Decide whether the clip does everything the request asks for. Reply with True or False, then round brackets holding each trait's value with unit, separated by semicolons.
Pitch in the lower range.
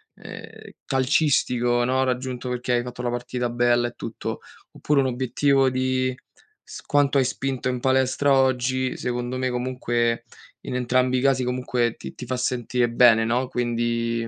True (125 Hz)